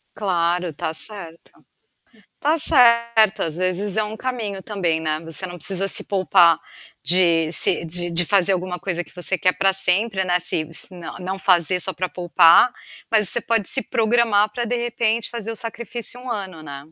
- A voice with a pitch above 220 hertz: No, high, 190 Hz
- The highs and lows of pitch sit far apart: No, average, 4.1 semitones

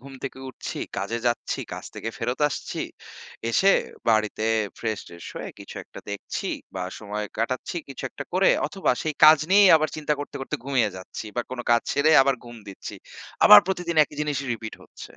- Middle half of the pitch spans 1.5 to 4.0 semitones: No, wide, 5.4 semitones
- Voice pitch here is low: Yes, low, 130 Hz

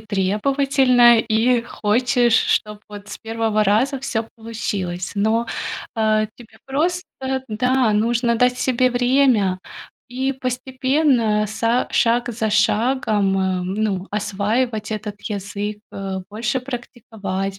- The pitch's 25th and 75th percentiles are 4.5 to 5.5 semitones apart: No, average, 3.2 semitones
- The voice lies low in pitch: No, high, 225 Hz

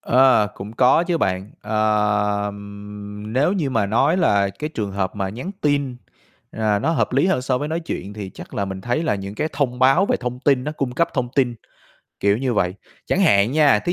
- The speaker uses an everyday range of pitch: No, wide, 5.7 semitones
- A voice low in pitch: Yes, low, 125 Hz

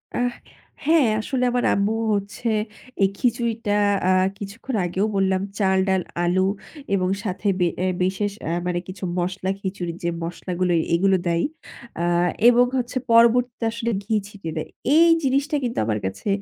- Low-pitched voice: No, high, 200 Hz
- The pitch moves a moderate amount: Yes, average, 4.2 semitones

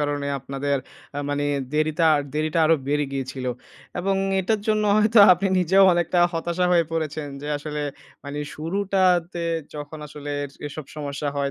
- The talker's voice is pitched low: No, medium, 155 Hz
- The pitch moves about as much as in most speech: Yes, average, 3.5 semitones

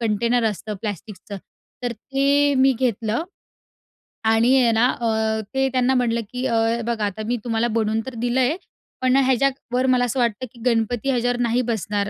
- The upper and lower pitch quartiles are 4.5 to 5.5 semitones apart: No, narrow, 2.5 semitones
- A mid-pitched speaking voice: No, high, 240 Hz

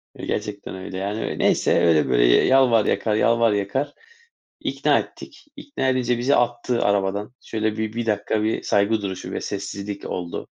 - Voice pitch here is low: Yes, low, 105 Hz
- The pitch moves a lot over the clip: No, average, 3.0 semitones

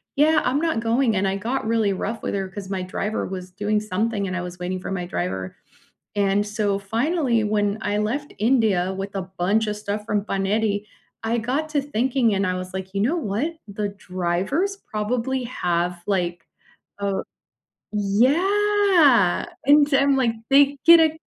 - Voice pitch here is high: Yes, high, 210 Hz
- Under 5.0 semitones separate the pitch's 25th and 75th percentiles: No, wide, 5.5 semitones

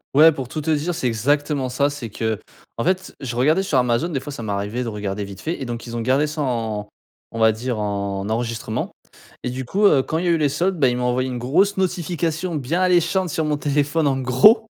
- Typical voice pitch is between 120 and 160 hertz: Yes, low, 135 Hz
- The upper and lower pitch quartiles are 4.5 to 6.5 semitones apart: Yes, wide, 5.4 semitones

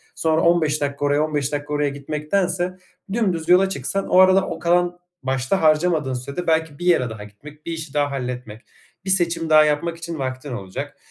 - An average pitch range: Yes, average, 3.7 semitones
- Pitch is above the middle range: No, medium, 155 Hz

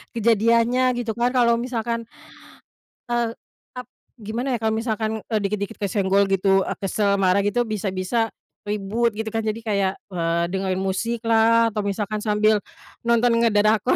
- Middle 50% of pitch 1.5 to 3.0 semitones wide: Yes, narrow, 2.5 semitones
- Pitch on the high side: Yes, high, 215 Hz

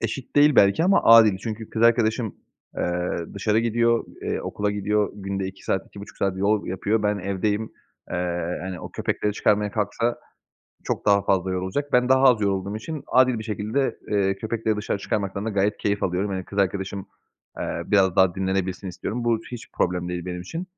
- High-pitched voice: No, low, 105 Hz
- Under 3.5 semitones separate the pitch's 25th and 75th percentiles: Yes, average, 2.9 semitones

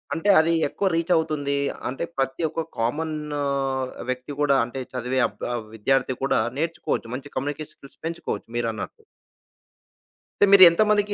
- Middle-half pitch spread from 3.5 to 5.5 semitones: Yes, average, 4.2 semitones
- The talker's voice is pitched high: No, medium, 145 Hz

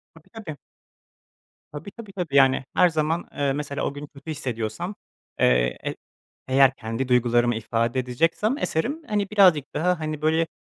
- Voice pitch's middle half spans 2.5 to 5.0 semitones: No, wide, 5.5 semitones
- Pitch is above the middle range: No, medium, 150 Hz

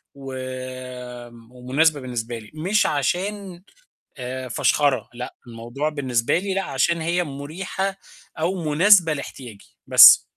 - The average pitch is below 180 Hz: Yes, medium, 140 Hz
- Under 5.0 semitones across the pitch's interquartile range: No, wide, 5.4 semitones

